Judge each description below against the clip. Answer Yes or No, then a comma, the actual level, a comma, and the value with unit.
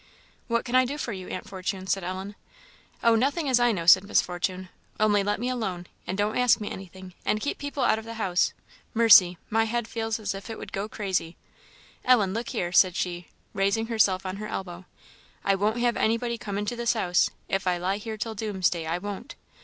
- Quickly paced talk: Yes, fast, 215 wpm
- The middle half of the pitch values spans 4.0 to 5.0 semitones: No, average, 3.5 semitones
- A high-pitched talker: Yes, high, 205 Hz